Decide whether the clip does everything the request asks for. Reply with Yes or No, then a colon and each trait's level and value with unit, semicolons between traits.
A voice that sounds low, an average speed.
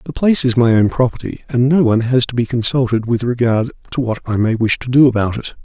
No: low, 120 Hz; fast, 255 wpm